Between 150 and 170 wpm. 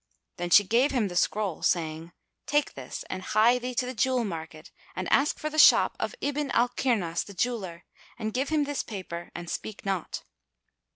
No: average, 190 wpm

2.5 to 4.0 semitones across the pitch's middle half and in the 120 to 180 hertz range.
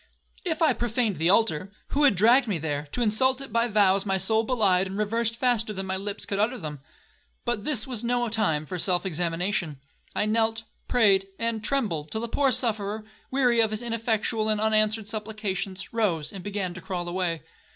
No: average, 3.5 semitones; high, 215 Hz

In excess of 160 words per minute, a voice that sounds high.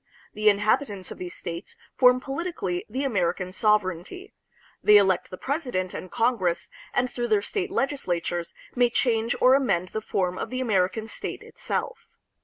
No: average, 155 wpm; high, 215 Hz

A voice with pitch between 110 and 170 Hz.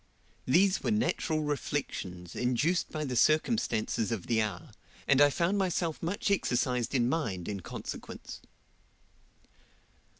Yes: medium, 140 Hz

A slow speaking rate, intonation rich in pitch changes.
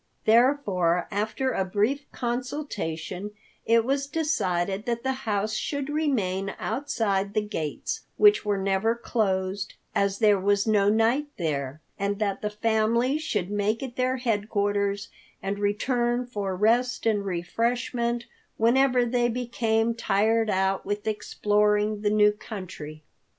No: slow, 130 wpm; average, 3.3 semitones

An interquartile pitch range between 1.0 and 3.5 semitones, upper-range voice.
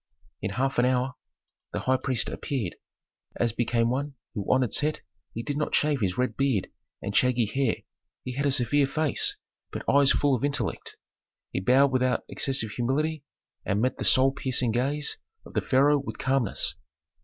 No: average, 2.8 semitones; low, 130 Hz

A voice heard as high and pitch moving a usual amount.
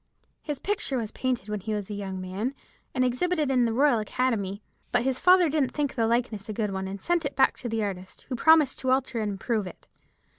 Yes: high, 240 Hz; average, 4.6 semitones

